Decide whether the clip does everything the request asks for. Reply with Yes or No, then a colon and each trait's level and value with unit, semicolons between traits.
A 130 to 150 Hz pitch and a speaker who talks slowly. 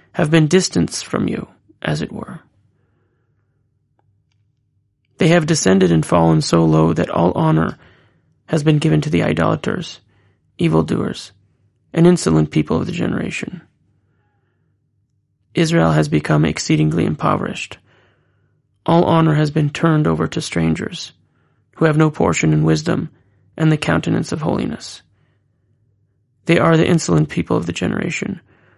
No: low, 110 Hz; slow, 130 wpm